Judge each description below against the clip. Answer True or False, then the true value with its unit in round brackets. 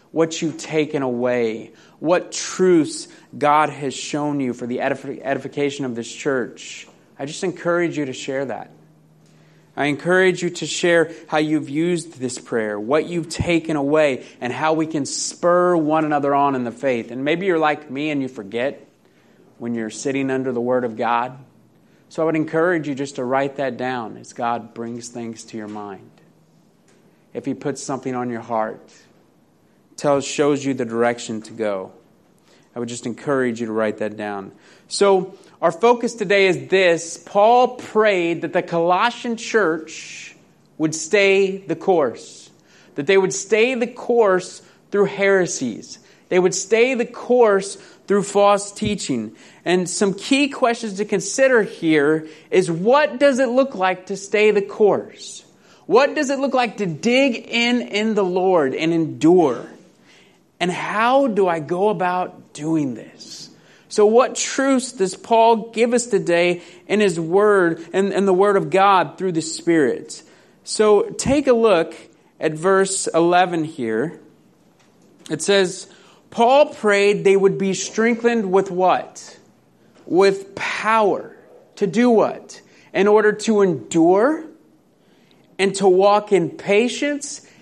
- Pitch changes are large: True (6.7 semitones)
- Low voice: False (180 Hz)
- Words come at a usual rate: True (155 wpm)